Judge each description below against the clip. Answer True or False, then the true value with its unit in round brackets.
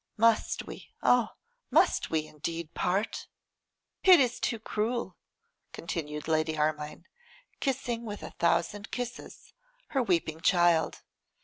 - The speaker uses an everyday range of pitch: False (6.7 semitones)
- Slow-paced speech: True (115 wpm)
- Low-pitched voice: False (185 Hz)